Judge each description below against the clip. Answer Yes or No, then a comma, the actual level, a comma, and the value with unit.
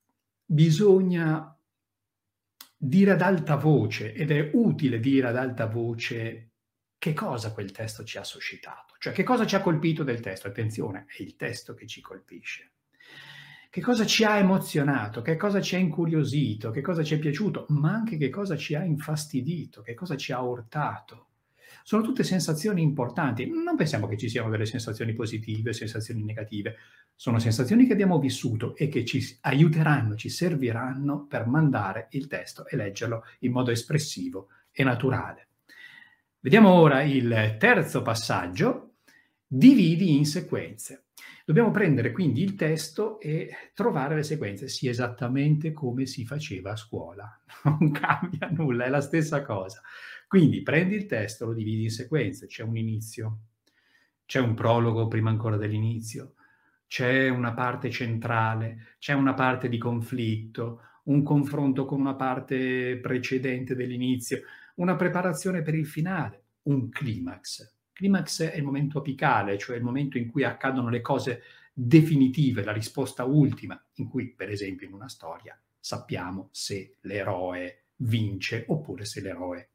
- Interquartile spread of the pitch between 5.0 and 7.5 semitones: Yes, wide, 5.5 semitones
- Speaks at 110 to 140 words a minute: No, average, 150 wpm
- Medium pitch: No, low, 130 Hz